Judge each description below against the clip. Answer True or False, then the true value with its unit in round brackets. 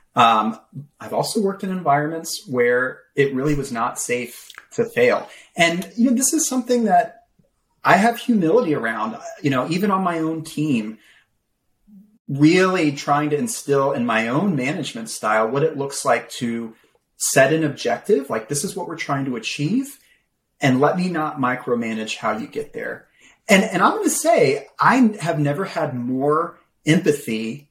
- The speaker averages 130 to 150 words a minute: False (170 wpm)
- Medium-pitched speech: True (160 Hz)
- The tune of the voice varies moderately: False (8.6 semitones)